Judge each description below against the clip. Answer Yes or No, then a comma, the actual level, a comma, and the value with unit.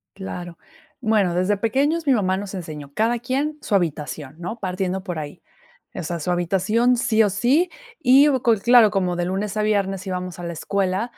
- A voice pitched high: Yes, high, 195 Hz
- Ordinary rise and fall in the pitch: Yes, average, 4.6 semitones